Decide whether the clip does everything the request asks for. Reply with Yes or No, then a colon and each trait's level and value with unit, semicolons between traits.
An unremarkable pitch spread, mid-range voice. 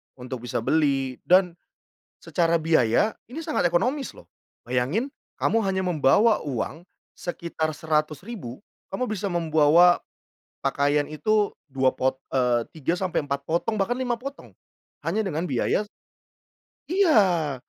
No: wide, 6.8 semitones; medium, 165 Hz